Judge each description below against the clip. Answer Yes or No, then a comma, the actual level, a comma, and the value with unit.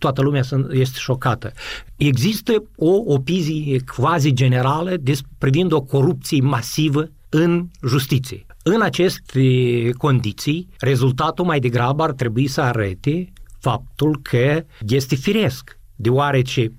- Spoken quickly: No, slow, 110 wpm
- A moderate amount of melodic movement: Yes, average, 3.5 semitones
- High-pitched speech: No, low, 135 Hz